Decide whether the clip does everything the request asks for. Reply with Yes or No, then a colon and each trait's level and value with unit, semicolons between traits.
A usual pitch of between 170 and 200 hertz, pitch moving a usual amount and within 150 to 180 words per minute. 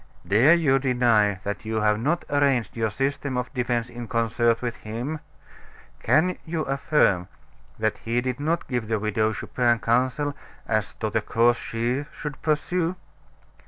No: low, 120 Hz; average, 4.2 semitones; average, 155 wpm